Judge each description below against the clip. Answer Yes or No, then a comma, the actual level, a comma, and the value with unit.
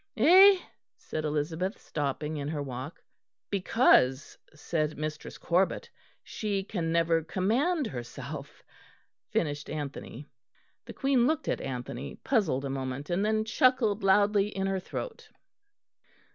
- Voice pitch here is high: No, medium, 170 Hz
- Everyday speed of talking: No, slow, 120 wpm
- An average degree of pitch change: No, wide, 6.7 semitones